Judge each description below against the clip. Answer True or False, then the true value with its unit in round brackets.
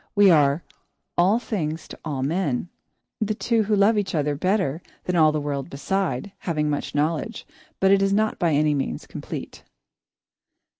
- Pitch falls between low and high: True (170 Hz)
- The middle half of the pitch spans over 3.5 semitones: True (5.2 semitones)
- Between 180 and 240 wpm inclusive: False (165 wpm)